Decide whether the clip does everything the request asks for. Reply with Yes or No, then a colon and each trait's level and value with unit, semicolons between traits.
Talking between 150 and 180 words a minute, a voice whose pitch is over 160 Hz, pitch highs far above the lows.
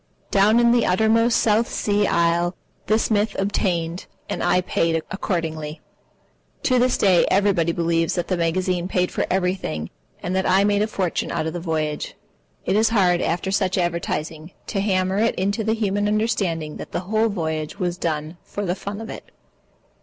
No: average, 175 wpm; medium, 185 Hz; average, 3.5 semitones